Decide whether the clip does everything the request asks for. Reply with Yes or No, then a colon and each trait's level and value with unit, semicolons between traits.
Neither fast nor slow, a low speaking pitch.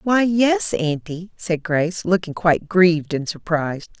No: average, 150 wpm; medium, 175 Hz